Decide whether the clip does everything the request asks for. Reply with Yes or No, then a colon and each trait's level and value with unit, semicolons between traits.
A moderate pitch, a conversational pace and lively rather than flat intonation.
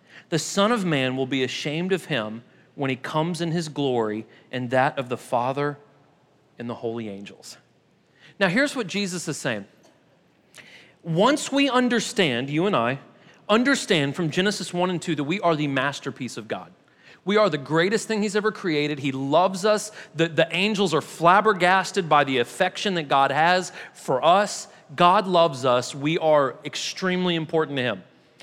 Yes: medium, 165 Hz; average, 175 wpm; wide, 5.9 semitones